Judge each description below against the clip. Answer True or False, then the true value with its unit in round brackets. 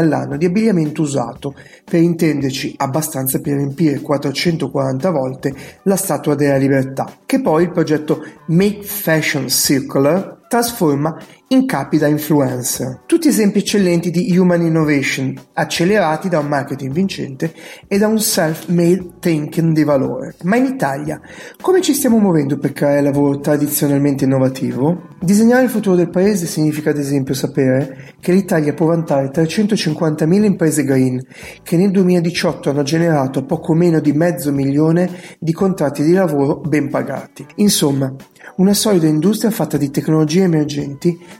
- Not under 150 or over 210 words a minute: False (140 wpm)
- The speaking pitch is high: False (160 Hz)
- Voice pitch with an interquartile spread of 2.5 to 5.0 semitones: True (4.1 semitones)